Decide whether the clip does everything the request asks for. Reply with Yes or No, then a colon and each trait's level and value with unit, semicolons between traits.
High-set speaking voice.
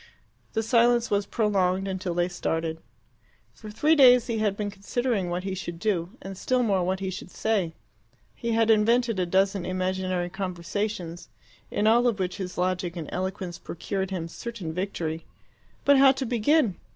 Yes: high, 195 Hz